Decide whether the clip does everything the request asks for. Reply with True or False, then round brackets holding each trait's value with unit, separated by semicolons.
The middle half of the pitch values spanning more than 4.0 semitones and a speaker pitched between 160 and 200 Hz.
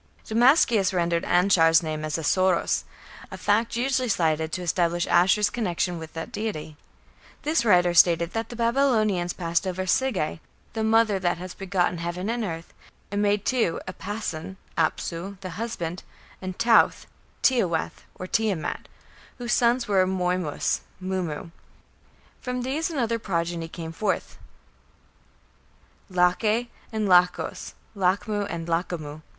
True (4.6 semitones; 185 Hz)